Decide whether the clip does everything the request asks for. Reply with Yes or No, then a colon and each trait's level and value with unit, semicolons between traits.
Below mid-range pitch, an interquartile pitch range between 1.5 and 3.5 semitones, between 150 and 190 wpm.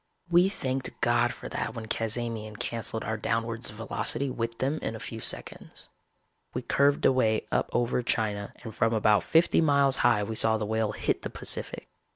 Yes: low, 115 Hz; average, 2.7 semitones; average, 180 wpm